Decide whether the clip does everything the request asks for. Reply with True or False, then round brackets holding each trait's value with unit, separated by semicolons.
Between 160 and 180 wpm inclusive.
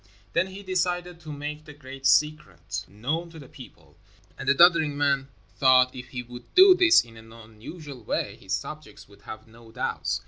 False (195 wpm)